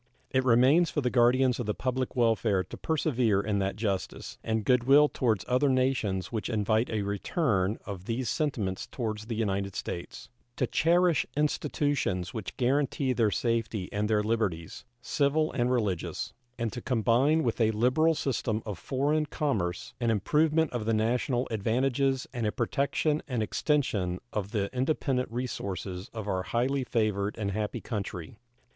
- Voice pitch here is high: No, low, 115 Hz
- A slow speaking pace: No, average, 160 wpm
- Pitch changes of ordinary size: Yes, average, 4.2 semitones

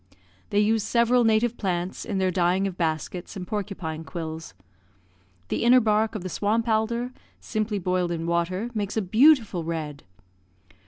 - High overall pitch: Yes, high, 195 Hz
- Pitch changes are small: No, average, 4.2 semitones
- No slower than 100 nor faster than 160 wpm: Yes, average, 155 wpm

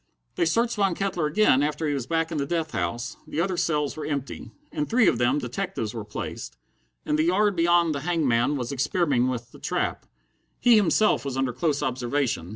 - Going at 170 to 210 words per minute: Yes, average, 200 wpm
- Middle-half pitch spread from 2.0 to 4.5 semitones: No, average, 5.2 semitones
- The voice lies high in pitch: No, medium, 150 Hz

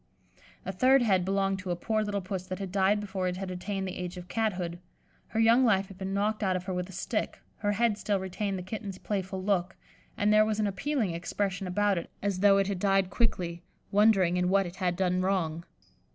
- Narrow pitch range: Yes, narrow, 2.1 semitones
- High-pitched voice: Yes, high, 195 Hz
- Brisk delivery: Yes, fast, 225 wpm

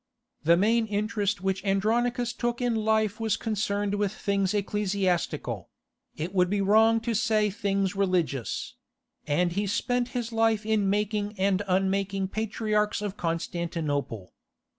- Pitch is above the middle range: Yes, high, 205 Hz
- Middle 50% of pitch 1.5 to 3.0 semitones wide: Yes, narrow, 2.4 semitones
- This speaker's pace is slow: Yes, slow, 125 wpm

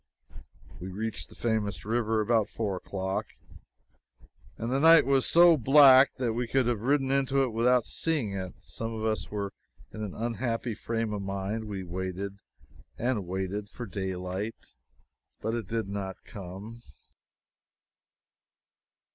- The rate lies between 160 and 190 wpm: No, average, 140 wpm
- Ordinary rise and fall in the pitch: Yes, average, 3.7 semitones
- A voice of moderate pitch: No, low, 110 Hz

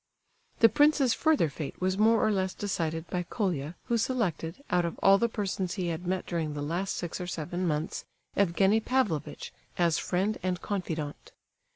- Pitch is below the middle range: No, medium, 185 Hz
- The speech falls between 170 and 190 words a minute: Yes, average, 175 wpm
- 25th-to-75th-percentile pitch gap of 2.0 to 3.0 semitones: No, average, 3.9 semitones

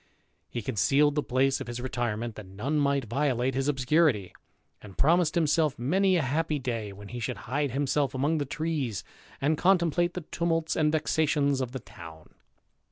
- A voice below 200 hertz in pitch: Yes, medium, 140 Hz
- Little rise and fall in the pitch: No, average, 4.5 semitones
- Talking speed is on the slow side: No, average, 175 wpm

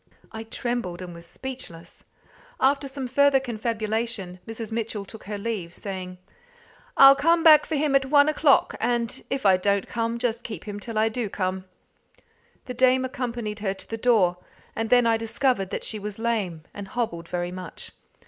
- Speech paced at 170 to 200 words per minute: Yes, average, 175 wpm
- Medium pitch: No, high, 225 Hz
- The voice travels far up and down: No, average, 4.3 semitones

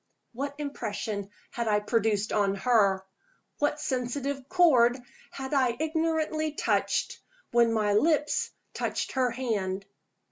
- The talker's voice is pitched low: No, high, 245 Hz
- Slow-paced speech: Yes, slow, 115 wpm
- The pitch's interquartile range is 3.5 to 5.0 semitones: No, wide, 5.5 semitones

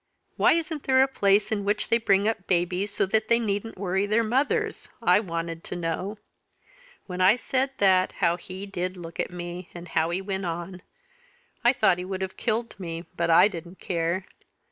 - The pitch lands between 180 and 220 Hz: Yes, high, 190 Hz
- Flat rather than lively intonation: No, average, 3.5 semitones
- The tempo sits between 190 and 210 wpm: Yes, average, 195 wpm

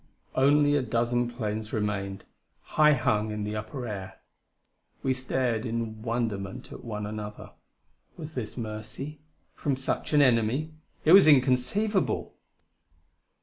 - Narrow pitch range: No, average, 4.1 semitones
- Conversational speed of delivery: No, slow, 125 wpm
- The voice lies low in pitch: Yes, low, 120 Hz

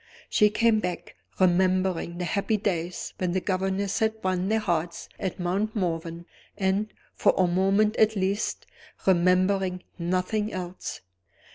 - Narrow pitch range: Yes, narrow, 2.3 semitones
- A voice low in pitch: No, medium, 185 Hz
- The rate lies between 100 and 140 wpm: Yes, slow, 135 wpm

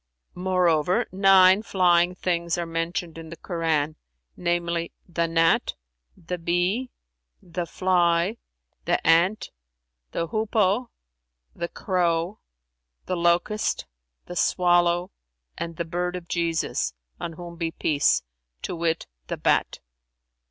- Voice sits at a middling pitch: Yes, medium, 175 Hz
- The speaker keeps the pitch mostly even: Yes, narrow, 1.6 semitones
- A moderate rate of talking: No, slow, 115 wpm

